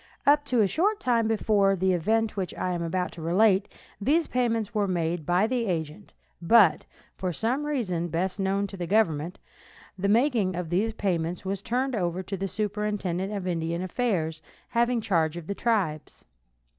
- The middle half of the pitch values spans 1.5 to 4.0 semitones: No, average, 4.4 semitones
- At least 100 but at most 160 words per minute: No, average, 175 wpm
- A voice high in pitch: Yes, high, 195 Hz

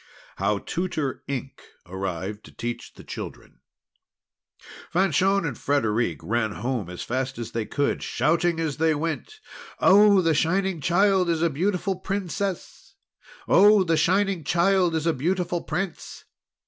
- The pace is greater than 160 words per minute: No, slow, 135 wpm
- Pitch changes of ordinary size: No, wide, 6.5 semitones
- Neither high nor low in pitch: Yes, medium, 165 Hz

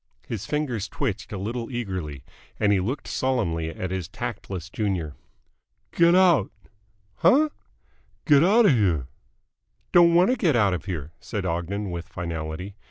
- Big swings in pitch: Yes, wide, 7.7 semitones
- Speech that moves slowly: No, average, 145 wpm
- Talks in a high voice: No, low, 100 Hz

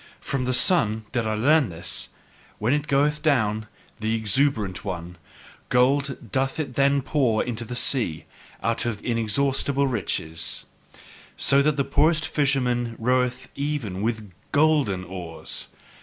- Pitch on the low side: Yes, low, 125 Hz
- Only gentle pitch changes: No, average, 4.4 semitones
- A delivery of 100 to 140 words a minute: Yes, slow, 135 wpm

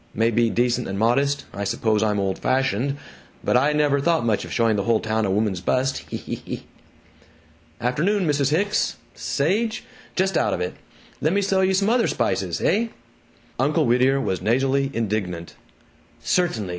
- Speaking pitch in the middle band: No, low, 130 Hz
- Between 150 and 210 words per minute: Yes, average, 170 wpm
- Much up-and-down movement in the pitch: Yes, wide, 6.0 semitones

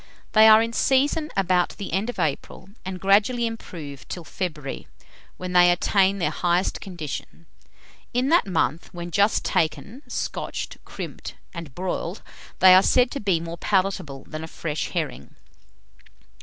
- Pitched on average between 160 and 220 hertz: Yes, medium, 185 Hz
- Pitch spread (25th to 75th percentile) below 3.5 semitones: No, average, 3.9 semitones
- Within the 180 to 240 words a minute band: No, average, 150 wpm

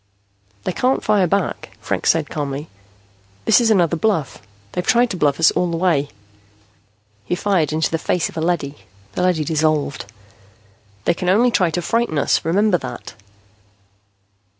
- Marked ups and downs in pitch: No, average, 4.0 semitones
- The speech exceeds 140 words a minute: Yes, average, 160 wpm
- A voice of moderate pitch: Yes, medium, 170 Hz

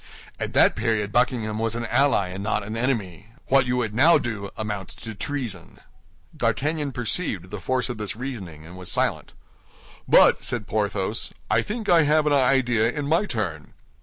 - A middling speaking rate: Yes, average, 175 wpm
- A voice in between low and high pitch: No, low, 115 Hz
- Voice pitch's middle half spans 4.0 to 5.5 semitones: Yes, average, 4.6 semitones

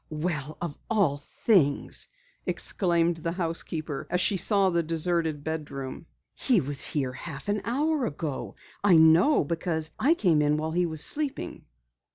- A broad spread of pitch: No, average, 3.5 semitones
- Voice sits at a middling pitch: Yes, medium, 165 Hz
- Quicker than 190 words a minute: No, average, 150 wpm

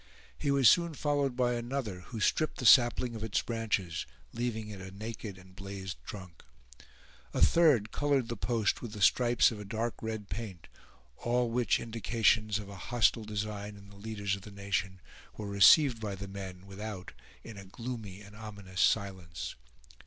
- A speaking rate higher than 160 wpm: Yes, average, 170 wpm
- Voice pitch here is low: Yes, low, 105 Hz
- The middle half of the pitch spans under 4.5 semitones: Yes, average, 3.2 semitones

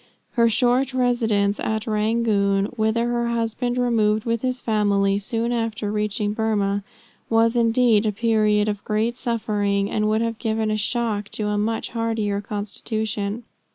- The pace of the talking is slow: No, average, 150 wpm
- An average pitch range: No, narrow, 1.9 semitones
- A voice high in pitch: Yes, high, 220 Hz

